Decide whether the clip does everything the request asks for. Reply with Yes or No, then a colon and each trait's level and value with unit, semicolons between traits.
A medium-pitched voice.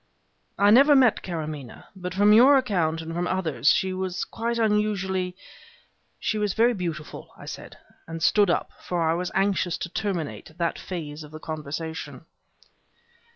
Yes: medium, 180 Hz